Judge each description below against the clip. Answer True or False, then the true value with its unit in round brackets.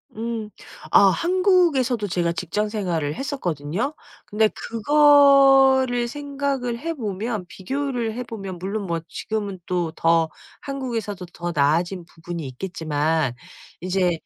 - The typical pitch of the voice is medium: False (210 Hz)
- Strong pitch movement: True (7.4 semitones)